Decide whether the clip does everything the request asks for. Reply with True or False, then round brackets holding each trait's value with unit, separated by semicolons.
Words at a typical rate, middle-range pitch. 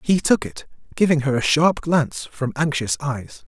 True (185 wpm; 145 Hz)